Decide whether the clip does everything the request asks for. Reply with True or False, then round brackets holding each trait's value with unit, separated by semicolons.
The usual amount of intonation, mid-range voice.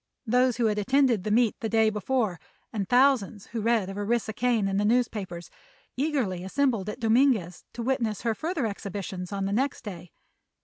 False (3.8 semitones; 220 Hz)